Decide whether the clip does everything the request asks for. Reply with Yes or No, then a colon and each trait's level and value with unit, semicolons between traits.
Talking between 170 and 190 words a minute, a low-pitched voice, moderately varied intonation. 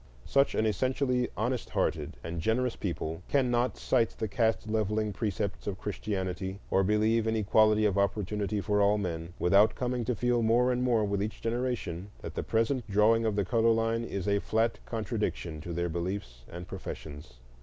Yes: average, 175 wpm; low, 105 Hz; average, 3.0 semitones